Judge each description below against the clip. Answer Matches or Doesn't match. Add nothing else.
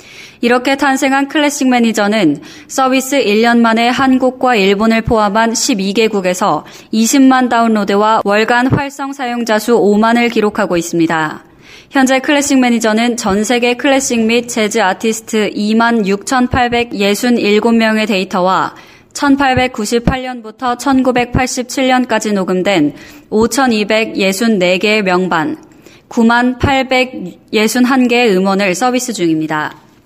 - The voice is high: Matches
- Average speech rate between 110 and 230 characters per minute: Matches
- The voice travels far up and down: Doesn't match